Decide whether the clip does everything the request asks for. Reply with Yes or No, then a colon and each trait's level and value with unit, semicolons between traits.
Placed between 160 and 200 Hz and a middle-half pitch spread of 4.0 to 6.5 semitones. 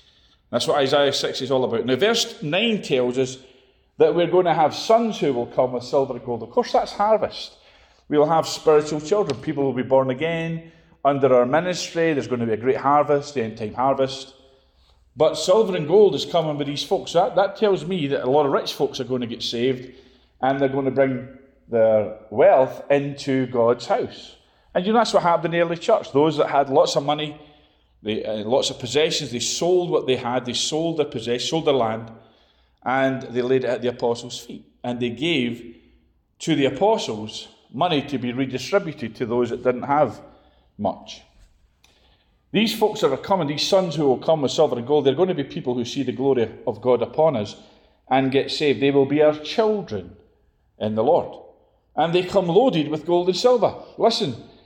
No: low, 135 Hz; average, 4.8 semitones